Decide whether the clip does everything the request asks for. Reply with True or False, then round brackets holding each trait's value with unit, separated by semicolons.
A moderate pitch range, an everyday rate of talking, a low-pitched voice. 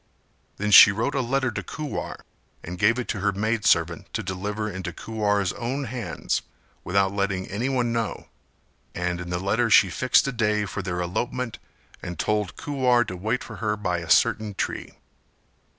True (4.1 semitones; 175 wpm; 105 Hz)